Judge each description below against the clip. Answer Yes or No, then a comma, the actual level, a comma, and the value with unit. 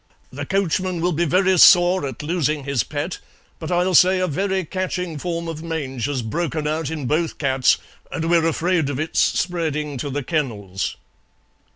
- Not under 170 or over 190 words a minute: Yes, average, 175 wpm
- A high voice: No, medium, 160 Hz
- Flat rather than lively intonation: No, average, 3.7 semitones